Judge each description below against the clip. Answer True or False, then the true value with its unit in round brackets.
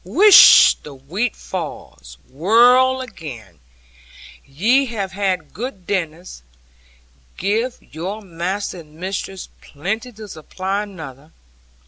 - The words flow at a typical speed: False (105 wpm)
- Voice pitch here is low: False (190 Hz)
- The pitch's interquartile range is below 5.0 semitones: False (5.6 semitones)